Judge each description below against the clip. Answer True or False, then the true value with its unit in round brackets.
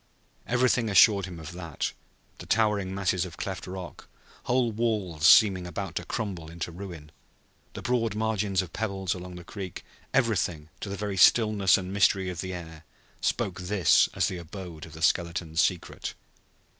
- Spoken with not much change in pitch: False (3.2 semitones)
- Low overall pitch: True (95 Hz)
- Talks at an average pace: True (165 wpm)